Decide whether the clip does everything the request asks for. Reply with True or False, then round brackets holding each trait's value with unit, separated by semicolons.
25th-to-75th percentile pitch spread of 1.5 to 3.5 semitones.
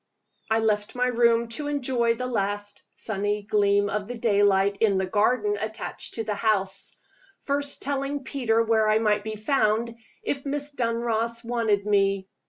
True (2.8 semitones)